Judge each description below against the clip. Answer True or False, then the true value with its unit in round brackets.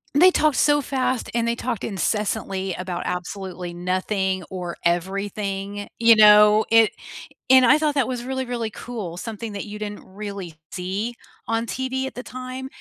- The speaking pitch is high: True (210 Hz)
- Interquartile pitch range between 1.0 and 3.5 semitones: False (4.5 semitones)